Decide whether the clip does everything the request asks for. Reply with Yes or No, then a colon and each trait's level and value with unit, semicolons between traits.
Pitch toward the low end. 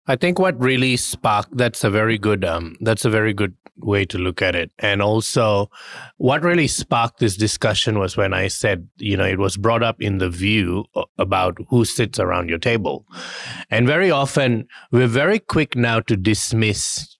Yes: low, 110 Hz